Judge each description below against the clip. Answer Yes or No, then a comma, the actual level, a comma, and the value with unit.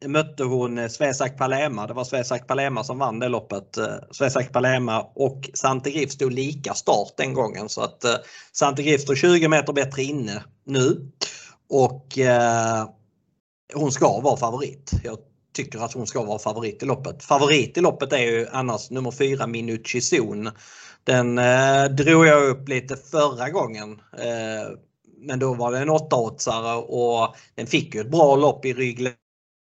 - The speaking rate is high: No, average, 155 wpm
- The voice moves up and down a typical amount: Yes, average, 3.1 semitones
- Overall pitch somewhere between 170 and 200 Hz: No, low, 130 Hz